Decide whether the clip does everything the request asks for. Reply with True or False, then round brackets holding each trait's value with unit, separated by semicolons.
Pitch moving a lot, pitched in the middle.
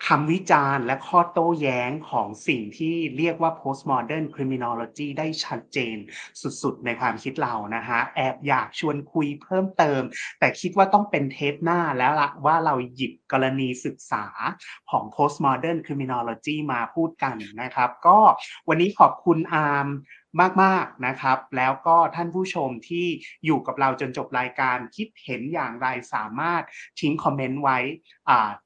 False (4.2 semitones; 145 Hz)